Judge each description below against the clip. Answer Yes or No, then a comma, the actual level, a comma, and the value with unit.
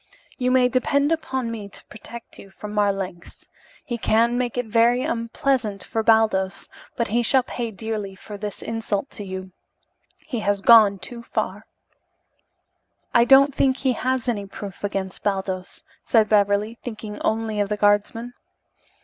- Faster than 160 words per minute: No, average, 155 wpm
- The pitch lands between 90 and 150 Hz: No, high, 220 Hz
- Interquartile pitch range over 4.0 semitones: No, average, 3.0 semitones